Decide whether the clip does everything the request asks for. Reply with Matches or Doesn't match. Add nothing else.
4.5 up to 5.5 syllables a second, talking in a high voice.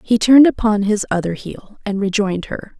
Matches